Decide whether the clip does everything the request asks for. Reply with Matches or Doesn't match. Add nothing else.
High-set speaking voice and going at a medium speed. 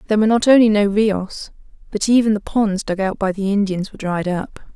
Doesn't match